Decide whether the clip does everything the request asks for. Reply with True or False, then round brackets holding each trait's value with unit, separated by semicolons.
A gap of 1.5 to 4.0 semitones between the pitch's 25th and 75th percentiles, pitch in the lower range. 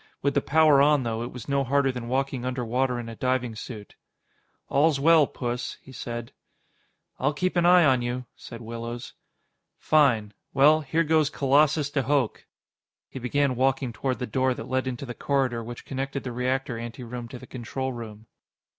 True (2.6 semitones; 130 Hz)